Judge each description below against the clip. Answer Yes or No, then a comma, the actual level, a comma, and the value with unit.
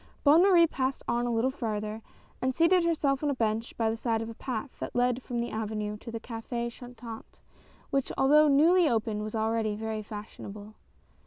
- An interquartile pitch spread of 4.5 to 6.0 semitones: No, average, 3.7 semitones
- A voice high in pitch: Yes, high, 235 Hz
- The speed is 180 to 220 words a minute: Yes, average, 190 wpm